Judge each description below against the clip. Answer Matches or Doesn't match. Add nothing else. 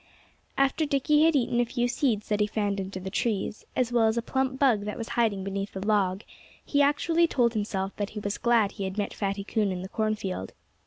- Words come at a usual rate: Doesn't match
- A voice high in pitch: Matches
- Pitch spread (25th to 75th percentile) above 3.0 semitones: Matches